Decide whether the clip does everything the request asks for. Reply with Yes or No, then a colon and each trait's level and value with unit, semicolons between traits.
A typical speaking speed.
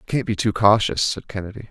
No: fast, 245 wpm